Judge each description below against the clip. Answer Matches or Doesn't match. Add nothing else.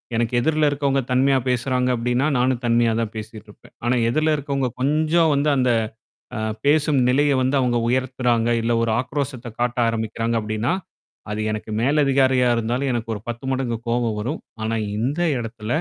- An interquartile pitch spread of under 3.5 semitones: Matches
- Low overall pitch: Matches